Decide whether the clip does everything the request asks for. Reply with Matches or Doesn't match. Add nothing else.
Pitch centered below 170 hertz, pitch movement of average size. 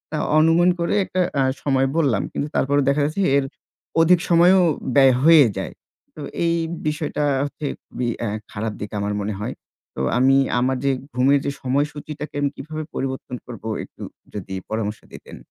Matches